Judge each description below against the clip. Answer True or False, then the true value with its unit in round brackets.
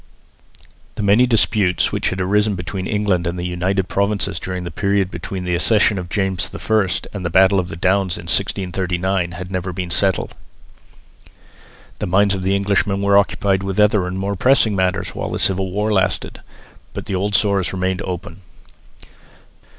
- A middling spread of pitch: False (1.7 semitones)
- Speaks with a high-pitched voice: False (95 Hz)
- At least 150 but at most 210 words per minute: True (170 wpm)